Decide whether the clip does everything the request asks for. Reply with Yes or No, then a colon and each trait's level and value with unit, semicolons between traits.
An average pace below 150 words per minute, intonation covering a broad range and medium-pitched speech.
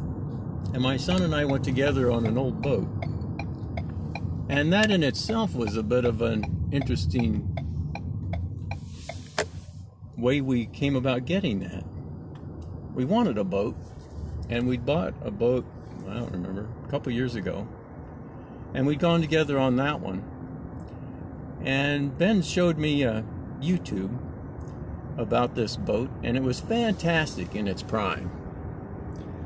No: slow, 135 wpm; wide, 7.1 semitones; low, 120 Hz